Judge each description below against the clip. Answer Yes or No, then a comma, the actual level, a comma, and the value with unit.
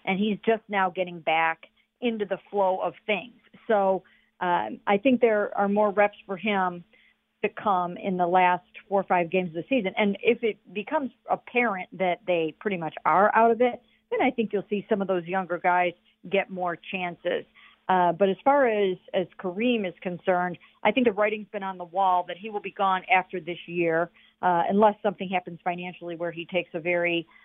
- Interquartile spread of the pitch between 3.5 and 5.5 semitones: No, average, 2.9 semitones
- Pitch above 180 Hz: Yes, high, 190 Hz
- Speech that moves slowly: No, fast, 205 wpm